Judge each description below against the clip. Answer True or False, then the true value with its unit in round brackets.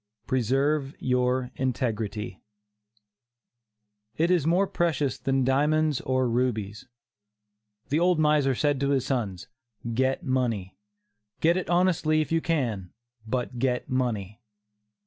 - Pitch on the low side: True (130 Hz)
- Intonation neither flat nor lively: True (3.9 semitones)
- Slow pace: True (115 wpm)